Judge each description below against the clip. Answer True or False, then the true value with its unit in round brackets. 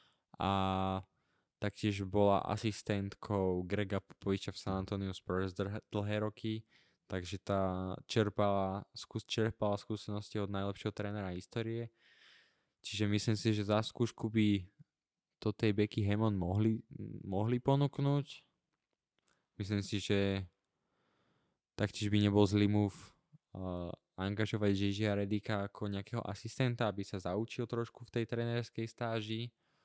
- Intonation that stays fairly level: True (2.1 semitones)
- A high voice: False (105 Hz)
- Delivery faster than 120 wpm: False (115 wpm)